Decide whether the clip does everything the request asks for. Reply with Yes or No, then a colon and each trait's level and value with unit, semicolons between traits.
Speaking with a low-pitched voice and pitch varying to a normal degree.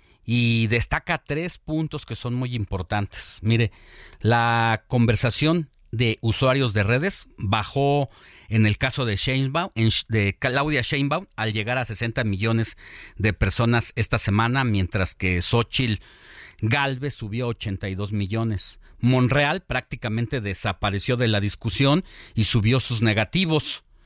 Yes: low, 115 Hz; average, 3.6 semitones